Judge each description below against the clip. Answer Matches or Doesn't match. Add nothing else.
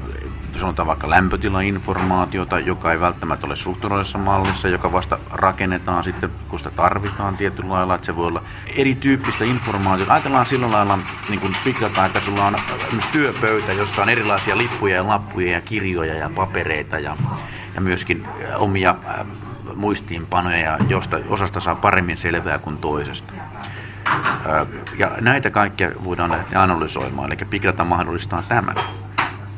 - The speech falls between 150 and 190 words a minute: Doesn't match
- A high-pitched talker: Doesn't match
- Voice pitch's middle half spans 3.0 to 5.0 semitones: Doesn't match